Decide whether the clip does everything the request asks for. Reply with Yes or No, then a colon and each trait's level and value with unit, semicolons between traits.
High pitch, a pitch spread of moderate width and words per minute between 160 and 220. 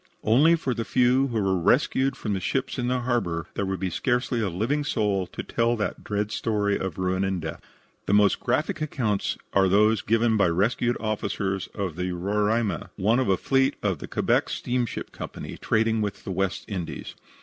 No: low, 105 Hz; average, 4.0 semitones; average, 195 wpm